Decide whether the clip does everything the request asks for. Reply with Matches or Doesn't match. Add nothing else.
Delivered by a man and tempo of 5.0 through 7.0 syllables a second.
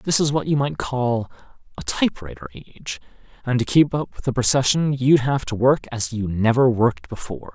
Matches